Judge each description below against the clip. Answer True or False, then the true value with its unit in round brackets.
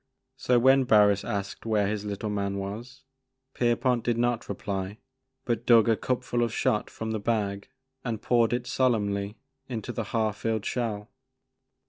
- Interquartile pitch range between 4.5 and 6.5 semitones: False (2.8 semitones)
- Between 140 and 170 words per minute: True (160 wpm)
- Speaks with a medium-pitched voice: False (110 Hz)